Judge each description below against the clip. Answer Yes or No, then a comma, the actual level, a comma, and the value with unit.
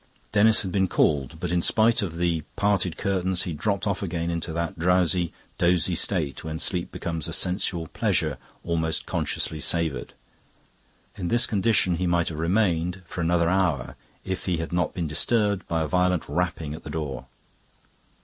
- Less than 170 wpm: No, average, 175 wpm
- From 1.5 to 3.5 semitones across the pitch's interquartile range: Yes, narrow, 2.5 semitones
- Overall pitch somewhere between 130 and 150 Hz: No, very low, 85 Hz